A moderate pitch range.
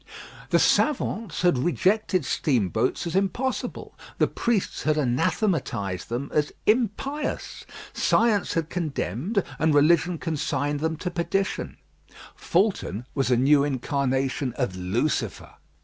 No: wide, 6.3 semitones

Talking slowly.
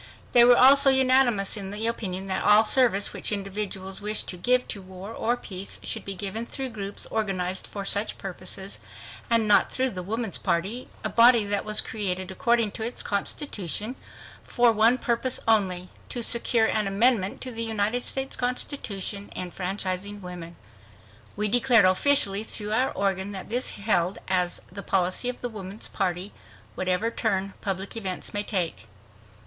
No: average, 155 wpm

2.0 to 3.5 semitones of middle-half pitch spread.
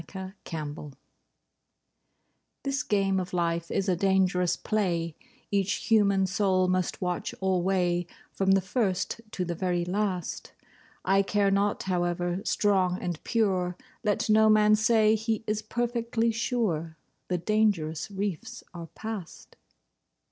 Yes: average, 3.1 semitones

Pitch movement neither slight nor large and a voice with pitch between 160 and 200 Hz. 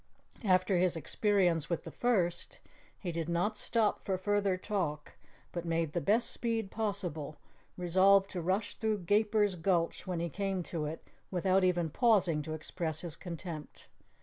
Yes: average, 3.4 semitones; medium, 185 Hz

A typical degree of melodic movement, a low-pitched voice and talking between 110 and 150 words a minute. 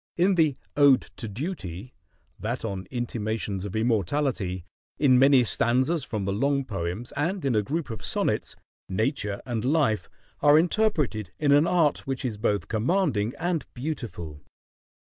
No: wide, 5.7 semitones; low, 125 Hz; average, 145 wpm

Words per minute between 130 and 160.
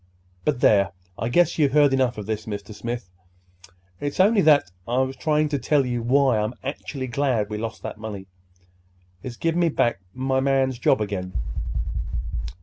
No: average, 170 wpm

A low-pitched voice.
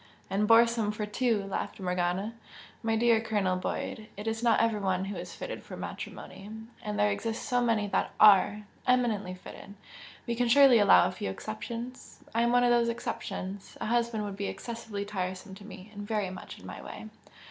No: high, 210 Hz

